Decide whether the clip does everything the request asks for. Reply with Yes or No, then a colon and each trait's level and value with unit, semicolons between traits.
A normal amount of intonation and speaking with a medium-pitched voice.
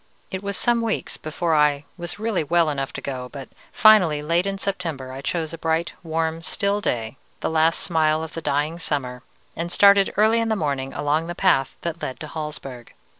Yes: average, 4.1 semitones; medium, 160 Hz